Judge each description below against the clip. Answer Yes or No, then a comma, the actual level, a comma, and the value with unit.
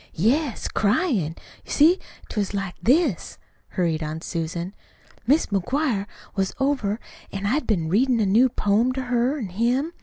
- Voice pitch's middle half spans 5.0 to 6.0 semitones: Yes, wide, 5.6 semitones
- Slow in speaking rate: No, average, 155 wpm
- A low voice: No, high, 220 Hz